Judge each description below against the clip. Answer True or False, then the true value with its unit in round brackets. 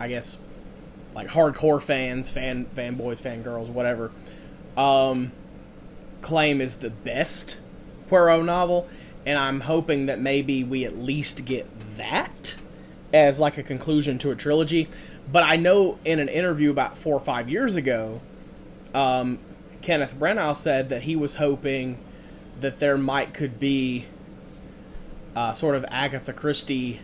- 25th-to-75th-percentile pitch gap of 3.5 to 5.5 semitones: False (2.9 semitones)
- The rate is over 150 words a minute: False (140 wpm)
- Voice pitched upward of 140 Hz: False (135 Hz)